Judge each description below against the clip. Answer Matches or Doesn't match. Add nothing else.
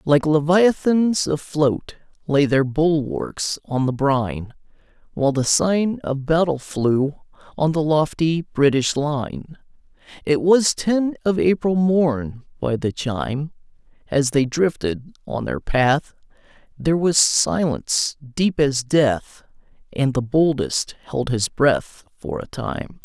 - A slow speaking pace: Matches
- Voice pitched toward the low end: Doesn't match